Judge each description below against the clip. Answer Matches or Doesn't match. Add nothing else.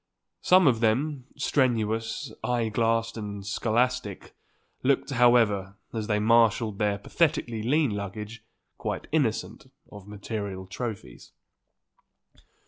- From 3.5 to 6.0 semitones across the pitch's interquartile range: Doesn't match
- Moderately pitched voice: Doesn't match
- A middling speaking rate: Doesn't match